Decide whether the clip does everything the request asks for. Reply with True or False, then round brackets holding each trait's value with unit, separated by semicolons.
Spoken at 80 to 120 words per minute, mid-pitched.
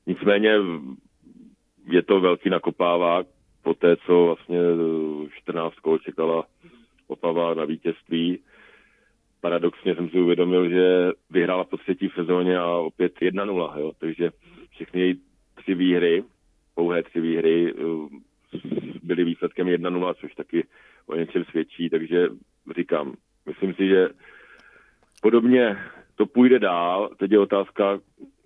False (115 wpm; 85 Hz)